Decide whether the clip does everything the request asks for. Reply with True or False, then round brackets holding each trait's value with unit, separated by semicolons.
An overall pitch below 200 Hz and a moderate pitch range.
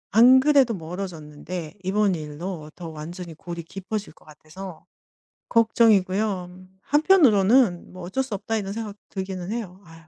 True (190 Hz; 4.2 semitones)